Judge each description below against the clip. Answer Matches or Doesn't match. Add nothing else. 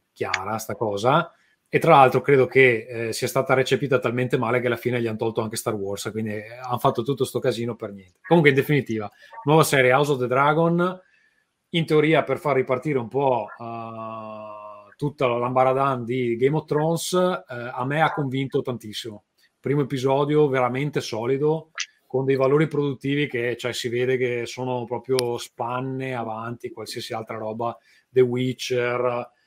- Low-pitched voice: Matches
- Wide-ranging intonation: Doesn't match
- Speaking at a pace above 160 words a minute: Matches